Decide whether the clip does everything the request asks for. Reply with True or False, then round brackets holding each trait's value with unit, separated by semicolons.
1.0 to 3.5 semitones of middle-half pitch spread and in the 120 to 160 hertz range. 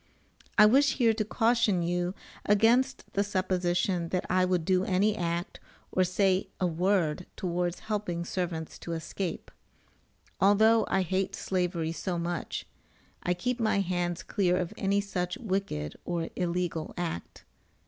False (2.5 semitones; 185 Hz)